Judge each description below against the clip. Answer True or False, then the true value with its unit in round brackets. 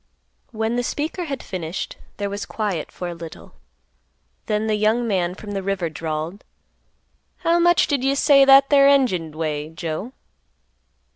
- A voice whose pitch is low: False (210 Hz)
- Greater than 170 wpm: False (160 wpm)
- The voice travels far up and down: True (8.1 semitones)